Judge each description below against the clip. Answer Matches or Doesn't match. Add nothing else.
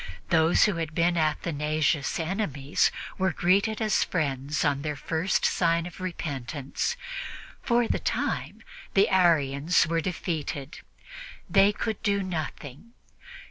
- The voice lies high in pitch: Doesn't match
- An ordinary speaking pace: Doesn't match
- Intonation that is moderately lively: Matches